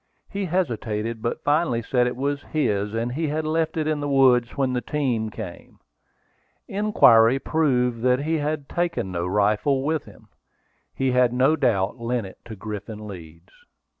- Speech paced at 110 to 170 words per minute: Yes, average, 165 wpm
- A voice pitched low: Yes, low, 125 Hz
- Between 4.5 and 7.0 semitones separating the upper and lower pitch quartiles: Yes, average, 5.2 semitones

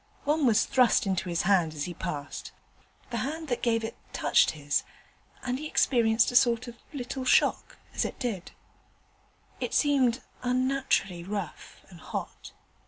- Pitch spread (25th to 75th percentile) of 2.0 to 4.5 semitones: No, wide, 5.5 semitones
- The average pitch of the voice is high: Yes, high, 235 Hz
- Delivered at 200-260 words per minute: No, average, 160 wpm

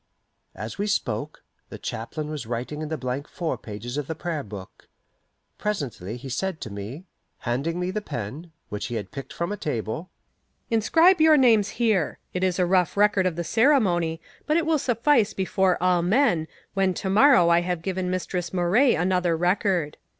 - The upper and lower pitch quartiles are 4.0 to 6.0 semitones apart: Yes, wide, 5.5 semitones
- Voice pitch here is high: No, medium, 175 Hz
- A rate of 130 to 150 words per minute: No, average, 180 wpm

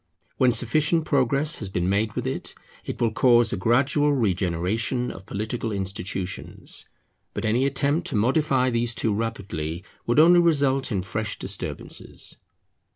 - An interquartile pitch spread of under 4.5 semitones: No, wide, 5.5 semitones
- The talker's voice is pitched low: Yes, low, 115 Hz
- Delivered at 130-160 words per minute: Yes, average, 145 wpm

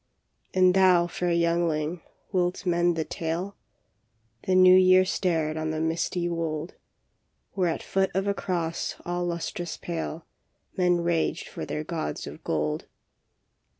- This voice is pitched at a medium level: Yes, medium, 170 Hz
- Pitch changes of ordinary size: No, narrow, 2.1 semitones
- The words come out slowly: No, average, 150 wpm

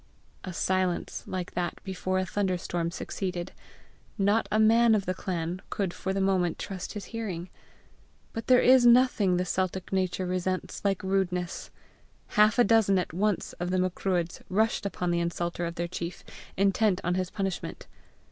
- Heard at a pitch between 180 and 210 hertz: Yes, medium, 185 Hz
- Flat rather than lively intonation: Yes, narrow, 2.2 semitones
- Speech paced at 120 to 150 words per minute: No, average, 165 wpm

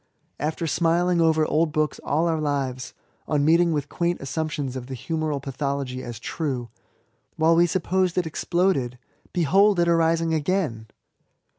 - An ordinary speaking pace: Yes, average, 145 wpm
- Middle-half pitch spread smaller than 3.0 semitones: No, average, 3.5 semitones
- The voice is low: No, medium, 160 Hz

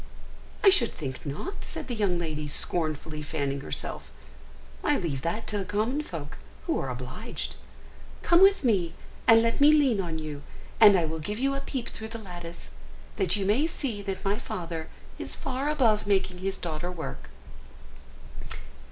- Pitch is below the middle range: No, high, 190 Hz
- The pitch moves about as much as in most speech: No, wide, 6.4 semitones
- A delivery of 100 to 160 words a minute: No, average, 170 wpm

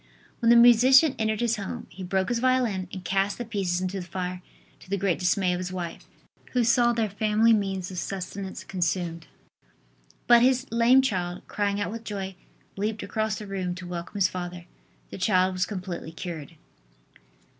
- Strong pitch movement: No, average, 3.6 semitones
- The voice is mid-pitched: No, high, 195 Hz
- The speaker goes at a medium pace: Yes, average, 180 wpm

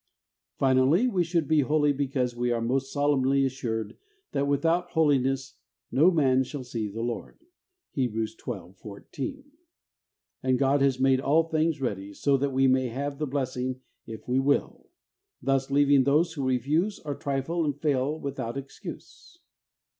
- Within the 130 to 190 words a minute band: Yes, average, 160 wpm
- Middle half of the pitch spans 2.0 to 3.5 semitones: Yes, narrow, 2.4 semitones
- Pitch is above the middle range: No, low, 135 Hz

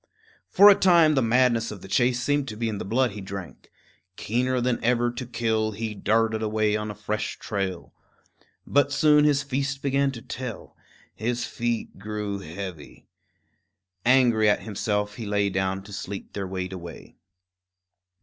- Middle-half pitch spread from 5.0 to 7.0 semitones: No, average, 3.7 semitones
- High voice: No, low, 110 Hz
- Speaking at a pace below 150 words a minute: No, average, 165 wpm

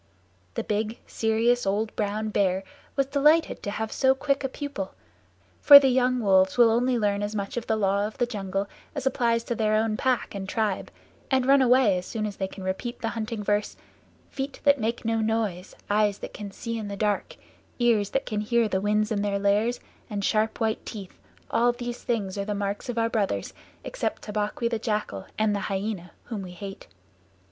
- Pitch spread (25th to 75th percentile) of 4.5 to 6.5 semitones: No, average, 2.9 semitones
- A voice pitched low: No, high, 215 Hz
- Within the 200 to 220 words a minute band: Yes, fast, 205 wpm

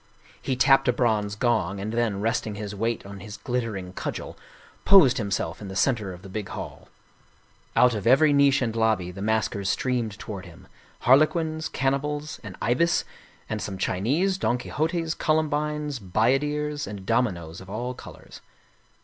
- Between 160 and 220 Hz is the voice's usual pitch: No, low, 115 Hz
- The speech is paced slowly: No, average, 160 wpm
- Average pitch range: No, wide, 5.7 semitones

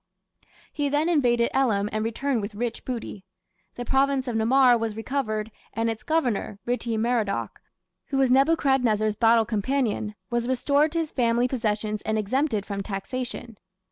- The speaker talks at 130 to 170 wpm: Yes, average, 150 wpm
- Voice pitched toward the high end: Yes, high, 235 Hz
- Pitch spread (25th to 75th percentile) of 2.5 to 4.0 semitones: Yes, average, 3.7 semitones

